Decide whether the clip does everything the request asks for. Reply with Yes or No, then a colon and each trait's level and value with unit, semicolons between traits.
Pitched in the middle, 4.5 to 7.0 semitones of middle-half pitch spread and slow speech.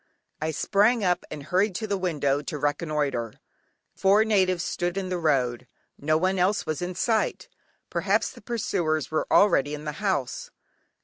No: medium, 175 Hz; average, 4.8 semitones; average, 165 wpm